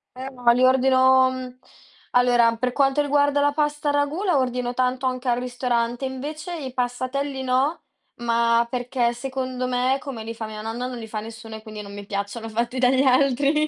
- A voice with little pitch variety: Yes, narrow, 2.2 semitones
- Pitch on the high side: Yes, very high, 255 Hz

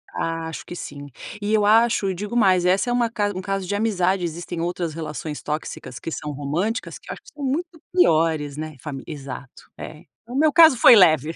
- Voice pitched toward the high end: No, medium, 180 Hz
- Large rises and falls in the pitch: Yes, wide, 5.9 semitones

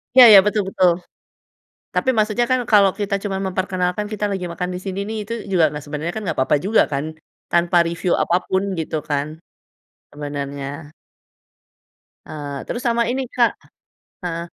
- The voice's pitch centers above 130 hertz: Yes, medium, 185 Hz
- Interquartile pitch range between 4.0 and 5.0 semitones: Yes, average, 4.7 semitones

